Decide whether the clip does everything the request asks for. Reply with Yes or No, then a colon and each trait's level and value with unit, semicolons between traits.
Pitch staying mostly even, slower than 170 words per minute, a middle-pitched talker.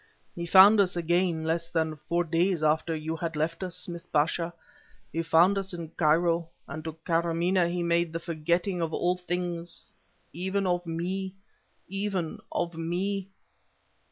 Yes: narrow, 1.7 semitones; average, 155 wpm; medium, 170 Hz